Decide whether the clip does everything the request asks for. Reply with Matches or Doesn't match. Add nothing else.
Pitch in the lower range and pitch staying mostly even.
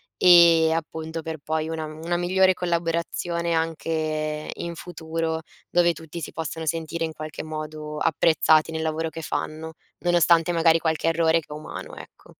Doesn't match